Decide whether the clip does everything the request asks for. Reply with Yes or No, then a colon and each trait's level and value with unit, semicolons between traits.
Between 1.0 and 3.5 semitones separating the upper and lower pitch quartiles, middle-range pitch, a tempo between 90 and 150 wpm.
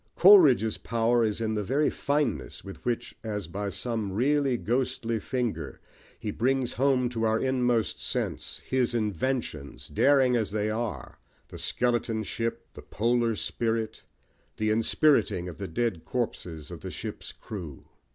No: average, 2.7 semitones; low, 115 Hz; average, 145 wpm